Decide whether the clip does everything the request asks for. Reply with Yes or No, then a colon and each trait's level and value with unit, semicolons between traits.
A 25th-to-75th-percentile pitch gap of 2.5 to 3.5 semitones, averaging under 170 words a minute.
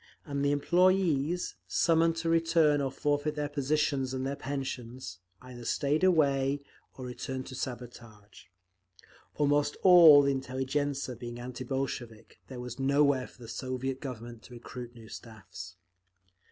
Yes: average, 2.9 semitones; average, 140 wpm